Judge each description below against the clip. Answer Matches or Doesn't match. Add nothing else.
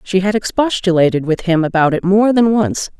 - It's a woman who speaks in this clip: Matches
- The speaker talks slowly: Doesn't match